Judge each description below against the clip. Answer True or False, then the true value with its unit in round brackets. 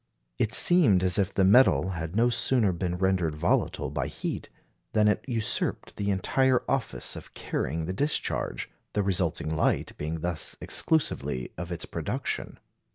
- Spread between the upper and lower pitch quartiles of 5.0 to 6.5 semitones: True (5.3 semitones)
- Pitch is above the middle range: False (95 Hz)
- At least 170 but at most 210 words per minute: False (155 wpm)